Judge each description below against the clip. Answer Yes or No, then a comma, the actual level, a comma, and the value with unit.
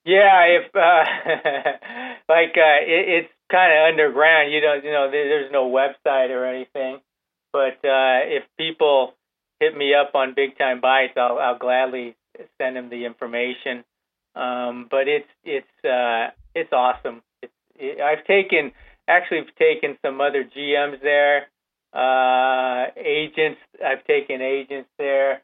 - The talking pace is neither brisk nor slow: Yes, average, 145 wpm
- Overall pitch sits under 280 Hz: Yes, medium, 140 Hz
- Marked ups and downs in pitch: No, average, 3.7 semitones